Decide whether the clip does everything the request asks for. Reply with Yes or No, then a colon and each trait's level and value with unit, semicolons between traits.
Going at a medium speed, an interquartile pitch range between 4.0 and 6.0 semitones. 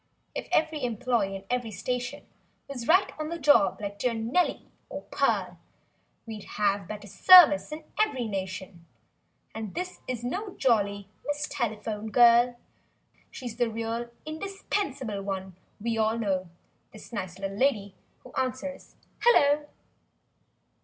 No: slow, 125 wpm; wide, 5.5 semitones